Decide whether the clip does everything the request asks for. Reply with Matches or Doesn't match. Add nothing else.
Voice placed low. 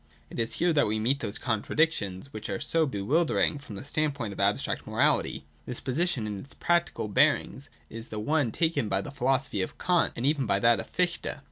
Matches